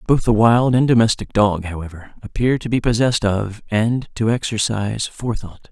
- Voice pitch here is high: No, low, 110 Hz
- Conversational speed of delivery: Yes, average, 170 wpm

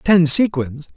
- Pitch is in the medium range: Yes, medium, 160 Hz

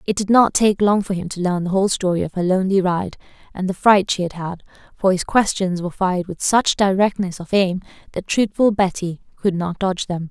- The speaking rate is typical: No, fast, 225 wpm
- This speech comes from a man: No, female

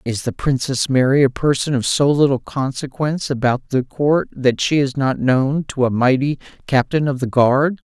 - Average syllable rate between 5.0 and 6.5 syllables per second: No, 4.7 syllables/s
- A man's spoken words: Yes, male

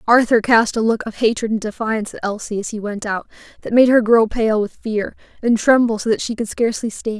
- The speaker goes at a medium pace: No, fast, 240 wpm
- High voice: Yes, high, 225 Hz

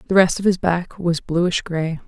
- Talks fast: Yes, fast, 230 wpm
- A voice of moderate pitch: Yes, medium, 175 Hz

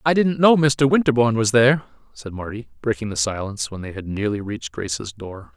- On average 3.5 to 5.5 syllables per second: No, 6.0 syllables/s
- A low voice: Yes, low, 115 Hz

